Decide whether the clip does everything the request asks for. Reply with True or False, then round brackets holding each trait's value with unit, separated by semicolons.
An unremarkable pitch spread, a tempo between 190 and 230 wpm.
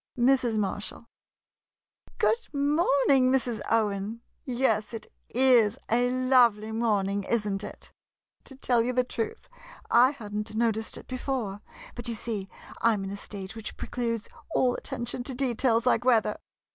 False (3.2 semitones; 150 wpm)